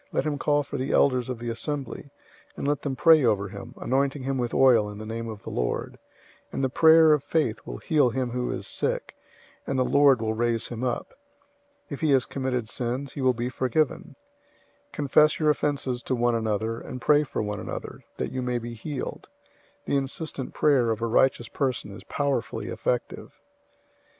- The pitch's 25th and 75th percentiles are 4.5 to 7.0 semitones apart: No, average, 3.3 semitones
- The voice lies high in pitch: No, low, 130 Hz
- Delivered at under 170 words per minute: No, average, 200 wpm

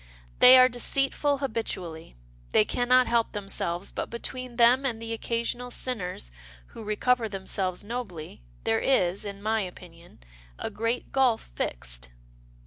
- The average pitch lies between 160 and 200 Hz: No, high, 225 Hz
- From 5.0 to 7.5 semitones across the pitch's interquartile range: Yes, wide, 5.5 semitones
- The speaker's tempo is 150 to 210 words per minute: No, average, 140 wpm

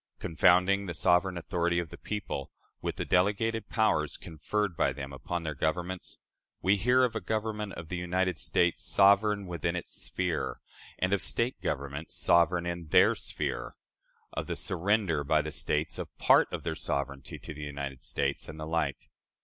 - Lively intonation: No, average, 4.3 semitones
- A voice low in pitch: Yes, very low, 85 Hz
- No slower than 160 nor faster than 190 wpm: Yes, average, 175 wpm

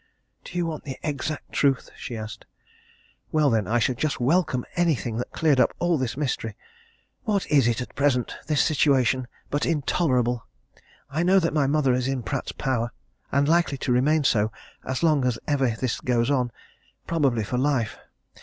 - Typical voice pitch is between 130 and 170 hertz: Yes, low, 135 Hz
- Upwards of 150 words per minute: Yes, average, 175 wpm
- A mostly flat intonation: No, average, 3.8 semitones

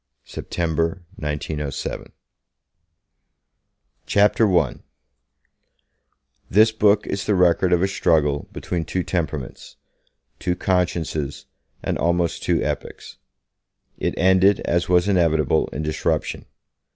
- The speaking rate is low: Yes, slow, 100 wpm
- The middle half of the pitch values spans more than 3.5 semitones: No, average, 3.1 semitones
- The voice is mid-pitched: No, very low, 85 Hz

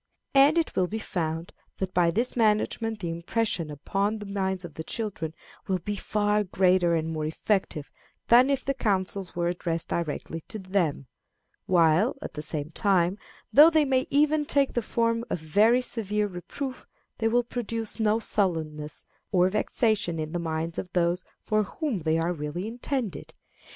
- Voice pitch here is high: Yes, high, 195 Hz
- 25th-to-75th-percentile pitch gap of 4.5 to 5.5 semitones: Yes, average, 5.2 semitones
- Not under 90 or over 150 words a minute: No, average, 170 wpm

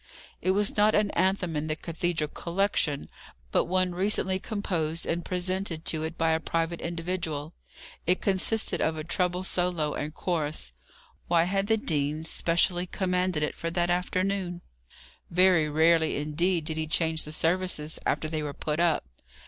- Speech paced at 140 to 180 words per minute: Yes, average, 160 wpm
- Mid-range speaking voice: Yes, medium, 170 Hz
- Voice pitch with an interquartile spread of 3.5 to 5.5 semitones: No, average, 2.8 semitones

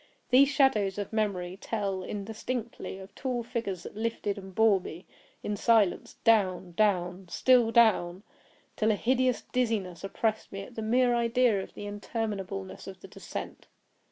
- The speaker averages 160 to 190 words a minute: No, average, 140 wpm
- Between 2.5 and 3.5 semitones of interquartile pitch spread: Yes, average, 3.2 semitones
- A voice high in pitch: Yes, high, 210 Hz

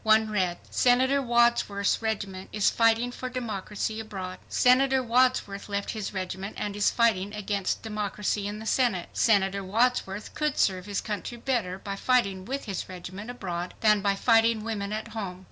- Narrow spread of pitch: No, average, 3.1 semitones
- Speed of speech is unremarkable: Yes, average, 160 wpm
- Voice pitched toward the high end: Yes, high, 210 Hz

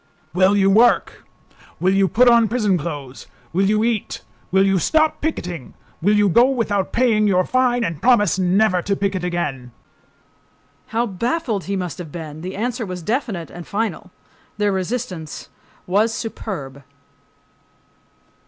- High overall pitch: Yes, high, 195 Hz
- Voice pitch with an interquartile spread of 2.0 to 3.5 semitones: No, average, 4.4 semitones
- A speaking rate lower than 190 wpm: Yes, slow, 135 wpm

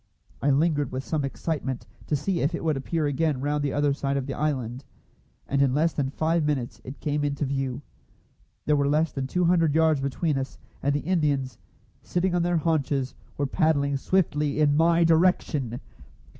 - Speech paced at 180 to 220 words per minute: Yes, average, 185 wpm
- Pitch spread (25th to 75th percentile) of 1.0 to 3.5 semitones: Yes, average, 2.8 semitones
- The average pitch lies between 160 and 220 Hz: No, medium, 145 Hz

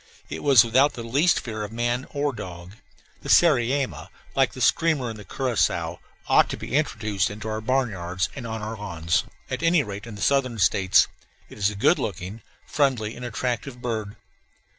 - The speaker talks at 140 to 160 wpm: No, average, 185 wpm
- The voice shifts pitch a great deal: No, average, 4.3 semitones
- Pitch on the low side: Yes, low, 115 Hz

